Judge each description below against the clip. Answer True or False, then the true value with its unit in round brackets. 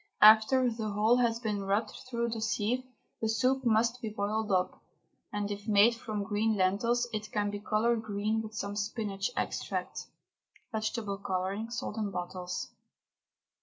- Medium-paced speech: True (155 wpm)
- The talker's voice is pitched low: False (215 Hz)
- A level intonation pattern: True (2.1 semitones)